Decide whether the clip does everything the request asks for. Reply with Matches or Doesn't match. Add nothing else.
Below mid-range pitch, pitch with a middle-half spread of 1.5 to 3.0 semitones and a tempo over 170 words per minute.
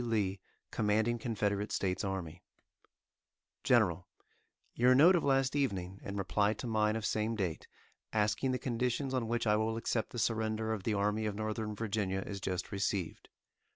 Doesn't match